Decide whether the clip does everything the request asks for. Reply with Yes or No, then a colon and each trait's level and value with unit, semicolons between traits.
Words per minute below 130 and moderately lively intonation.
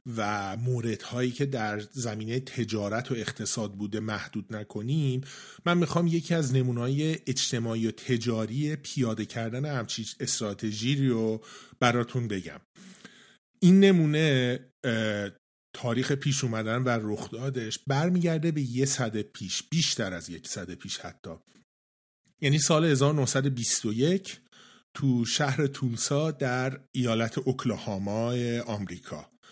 Yes: average, 110 wpm; average, 4.2 semitones